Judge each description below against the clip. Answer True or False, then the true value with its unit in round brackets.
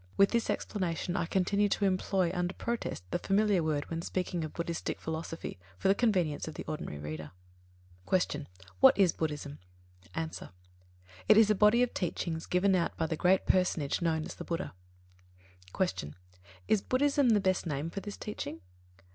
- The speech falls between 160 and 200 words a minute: True (175 wpm)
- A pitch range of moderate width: True (3.9 semitones)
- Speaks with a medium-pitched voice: True (180 Hz)